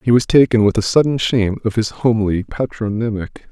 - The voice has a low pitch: Yes, low, 110 Hz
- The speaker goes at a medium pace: Yes, average, 190 wpm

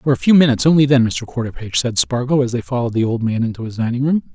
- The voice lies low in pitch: Yes, low, 125 Hz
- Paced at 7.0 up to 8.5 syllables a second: Yes, 7.3 syllables/s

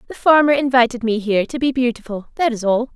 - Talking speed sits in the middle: No, fast, 225 wpm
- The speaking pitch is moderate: No, high, 245 Hz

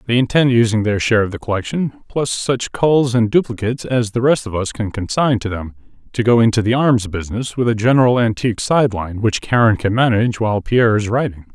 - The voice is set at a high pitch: No, low, 115 Hz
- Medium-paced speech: No, fast, 210 wpm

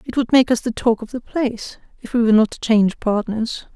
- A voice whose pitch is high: Yes, high, 230 Hz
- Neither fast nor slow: No, fast, 255 wpm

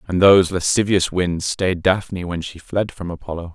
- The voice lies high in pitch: No, very low, 90 Hz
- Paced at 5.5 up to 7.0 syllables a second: No, 5.0 syllables/s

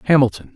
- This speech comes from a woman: No, male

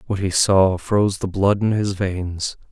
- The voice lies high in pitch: No, very low, 95 Hz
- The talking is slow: No, average, 200 wpm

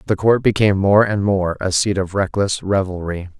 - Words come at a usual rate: Yes, average, 195 wpm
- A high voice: No, very low, 95 Hz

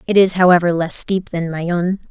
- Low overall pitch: No, medium, 175 Hz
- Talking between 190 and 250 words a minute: Yes, average, 200 wpm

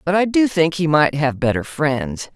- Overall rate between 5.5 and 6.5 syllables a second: No, 4.5 syllables/s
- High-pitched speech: No, medium, 155 Hz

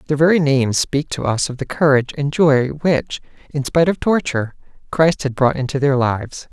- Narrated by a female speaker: No, male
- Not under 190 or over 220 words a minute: Yes, average, 200 wpm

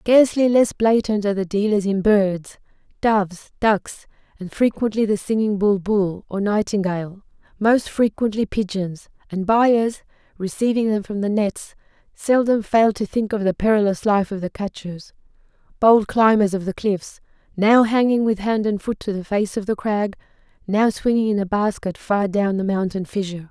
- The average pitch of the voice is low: No, high, 205 Hz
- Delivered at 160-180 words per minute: Yes, average, 165 wpm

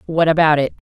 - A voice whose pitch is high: No, medium, 155 Hz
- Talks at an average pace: Yes, average, 190 wpm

